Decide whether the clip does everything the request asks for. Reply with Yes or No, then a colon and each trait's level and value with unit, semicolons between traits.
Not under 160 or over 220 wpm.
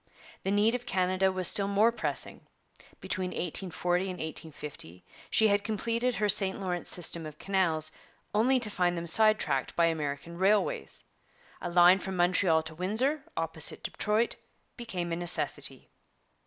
No: average, 150 wpm